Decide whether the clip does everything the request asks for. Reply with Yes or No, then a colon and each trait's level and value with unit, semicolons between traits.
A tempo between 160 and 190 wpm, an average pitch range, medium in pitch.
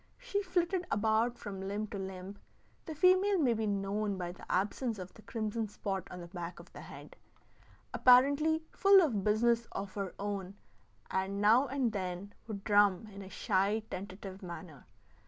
No: average, 170 wpm; average, 4.3 semitones; high, 205 Hz